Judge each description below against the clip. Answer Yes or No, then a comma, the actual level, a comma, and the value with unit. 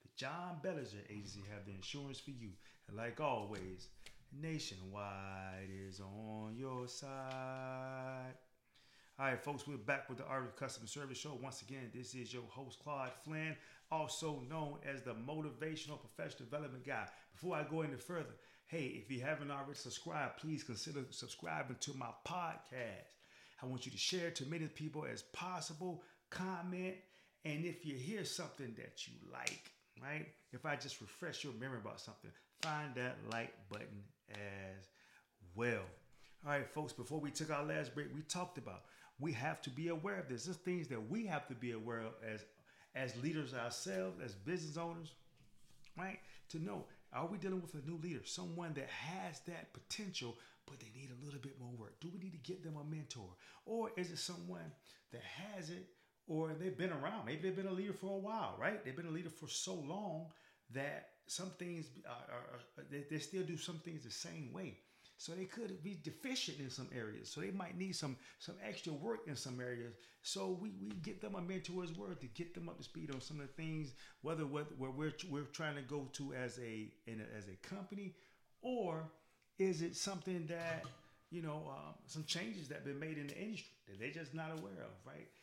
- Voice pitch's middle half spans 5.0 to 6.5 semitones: Yes, wide, 5.5 semitones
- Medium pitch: Yes, medium, 145 Hz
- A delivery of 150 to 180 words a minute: No, average, 195 wpm